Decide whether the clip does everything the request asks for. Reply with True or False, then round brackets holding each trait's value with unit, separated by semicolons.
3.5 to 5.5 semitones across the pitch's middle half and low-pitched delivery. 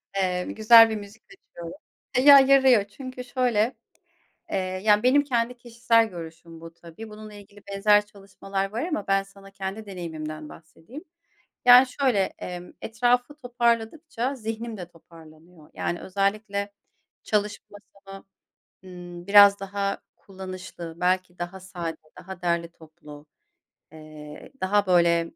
False (4.6 semitones; 200 Hz)